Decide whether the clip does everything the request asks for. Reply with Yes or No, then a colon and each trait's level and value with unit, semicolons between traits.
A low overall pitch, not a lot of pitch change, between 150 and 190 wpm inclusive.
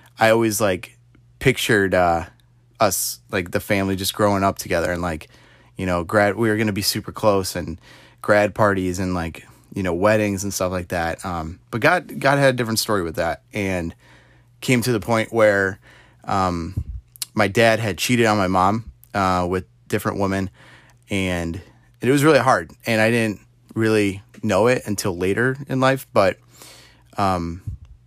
No: low, 105 Hz; average, 3.9 semitones; average, 175 wpm